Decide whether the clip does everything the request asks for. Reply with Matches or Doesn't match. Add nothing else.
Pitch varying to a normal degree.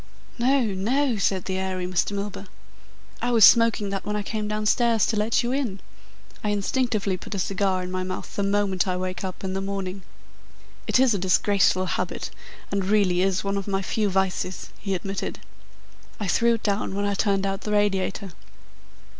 Doesn't match